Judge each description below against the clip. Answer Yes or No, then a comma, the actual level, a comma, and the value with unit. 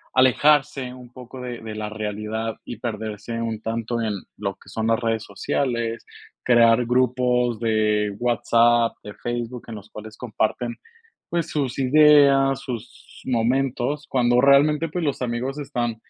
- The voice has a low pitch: Yes, low, 120 Hz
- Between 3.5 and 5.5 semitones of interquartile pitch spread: No, average, 2.7 semitones